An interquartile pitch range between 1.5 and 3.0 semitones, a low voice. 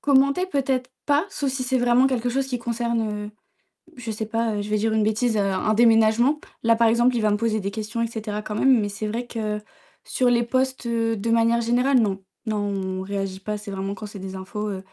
No: average, 2.7 semitones; high, 225 Hz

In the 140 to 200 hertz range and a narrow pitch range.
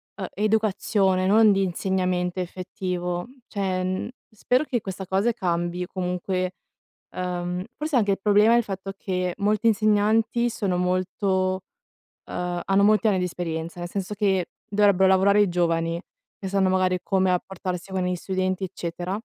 Yes: high, 190 Hz; narrow, 2.1 semitones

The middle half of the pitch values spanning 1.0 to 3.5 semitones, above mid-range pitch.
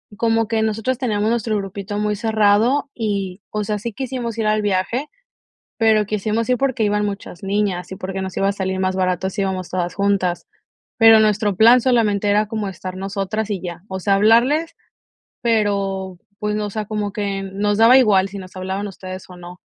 Yes: narrow, 2.4 semitones; high, 205 Hz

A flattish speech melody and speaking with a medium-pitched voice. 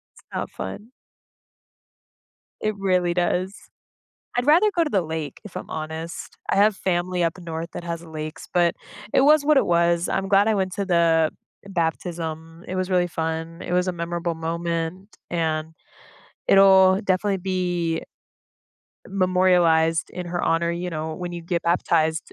Yes: narrow, 2.3 semitones; medium, 175 Hz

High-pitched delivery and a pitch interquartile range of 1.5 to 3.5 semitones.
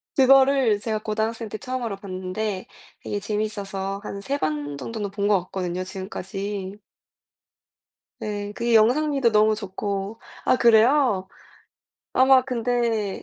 Yes: high, 210 Hz; average, 3.2 semitones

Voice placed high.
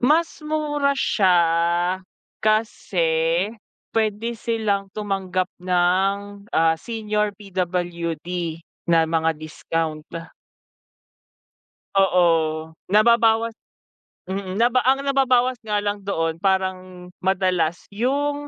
Yes: high, 200 Hz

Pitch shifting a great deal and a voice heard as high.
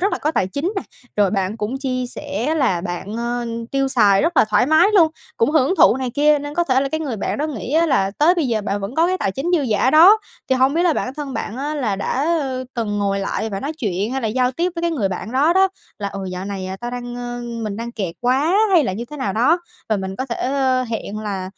Yes: wide, 6.2 semitones; very high, 250 Hz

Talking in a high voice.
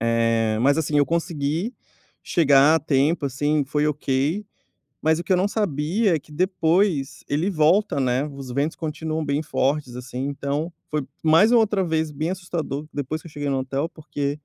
No: medium, 150 Hz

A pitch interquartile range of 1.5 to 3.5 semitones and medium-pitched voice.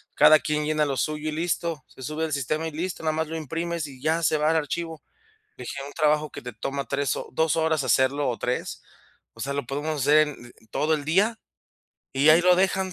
Yes: narrow, 2.4 semitones; medium, 155 Hz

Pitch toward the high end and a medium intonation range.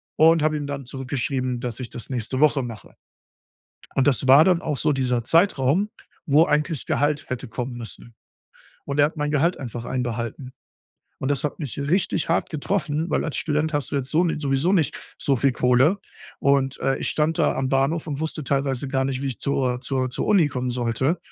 No: medium, 140 Hz; average, 3.1 semitones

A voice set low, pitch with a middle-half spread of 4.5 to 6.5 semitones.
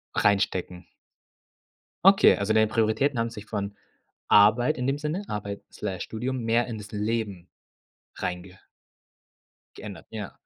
No: low, 110 Hz; average, 2.7 semitones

